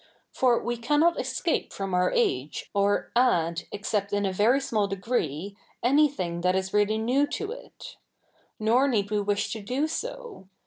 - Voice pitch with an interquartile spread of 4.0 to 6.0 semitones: Yes, average, 5.1 semitones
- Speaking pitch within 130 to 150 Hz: No, high, 210 Hz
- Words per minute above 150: Yes, average, 165 wpm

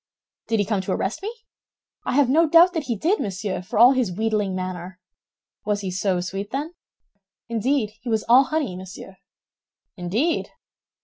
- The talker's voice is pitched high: Yes, high, 215 Hz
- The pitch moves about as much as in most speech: No, wide, 6.2 semitones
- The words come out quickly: No, average, 170 wpm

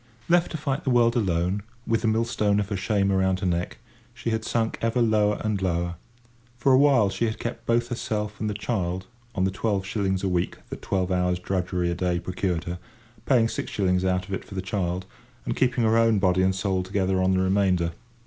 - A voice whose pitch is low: Yes, very low, 95 Hz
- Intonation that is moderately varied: Yes, average, 3.4 semitones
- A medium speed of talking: No, fast, 220 wpm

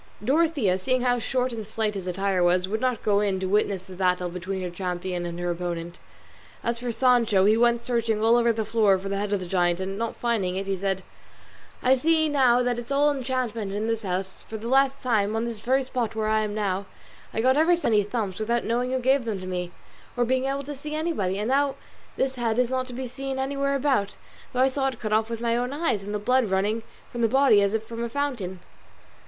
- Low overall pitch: No, high, 225 Hz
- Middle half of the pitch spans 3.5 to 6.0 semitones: Yes, average, 4.6 semitones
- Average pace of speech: No, fast, 245 wpm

